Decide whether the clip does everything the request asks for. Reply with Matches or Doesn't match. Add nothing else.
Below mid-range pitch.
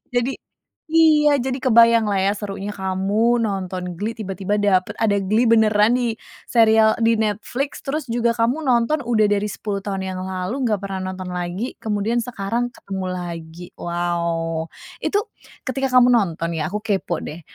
Doesn't match